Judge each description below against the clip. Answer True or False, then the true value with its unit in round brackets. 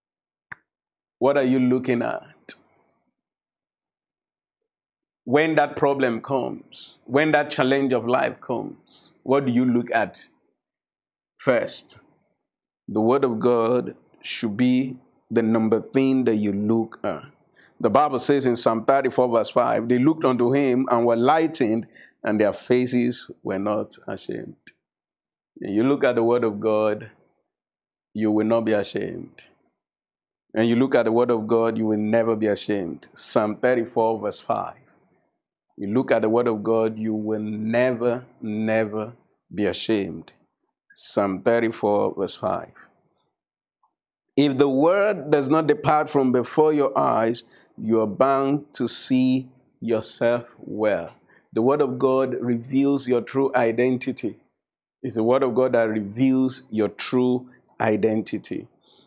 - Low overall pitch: True (120 Hz)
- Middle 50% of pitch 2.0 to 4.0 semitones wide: True (2.8 semitones)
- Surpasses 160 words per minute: False (140 wpm)